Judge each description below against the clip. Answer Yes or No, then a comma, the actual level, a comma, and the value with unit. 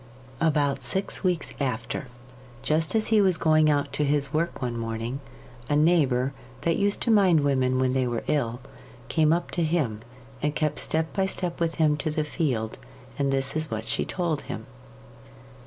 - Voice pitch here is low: No, medium, 150 Hz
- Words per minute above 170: Yes, average, 180 wpm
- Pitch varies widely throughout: No, average, 4.2 semitones